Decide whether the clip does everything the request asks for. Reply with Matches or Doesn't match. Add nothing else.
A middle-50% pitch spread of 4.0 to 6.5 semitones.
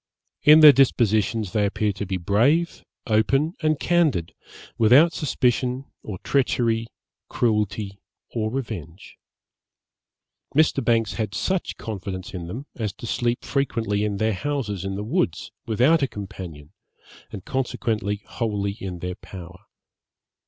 Matches